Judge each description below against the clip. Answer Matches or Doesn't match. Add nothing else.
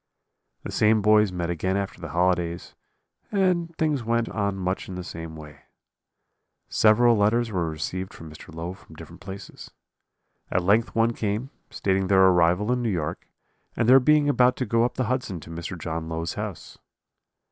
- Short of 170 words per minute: Doesn't match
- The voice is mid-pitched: Doesn't match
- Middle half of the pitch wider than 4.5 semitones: Matches